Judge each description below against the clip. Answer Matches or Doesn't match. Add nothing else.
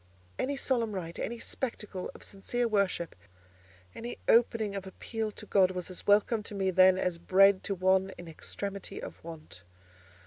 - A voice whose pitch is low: Doesn't match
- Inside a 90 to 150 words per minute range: Doesn't match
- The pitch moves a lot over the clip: Doesn't match